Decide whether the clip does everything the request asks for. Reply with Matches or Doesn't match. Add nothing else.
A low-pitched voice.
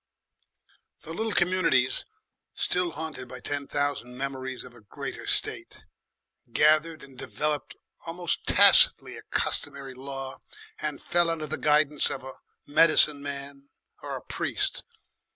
Doesn't match